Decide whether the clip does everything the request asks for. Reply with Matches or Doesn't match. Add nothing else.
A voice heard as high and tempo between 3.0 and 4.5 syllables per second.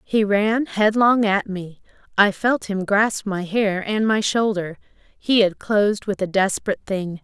Matches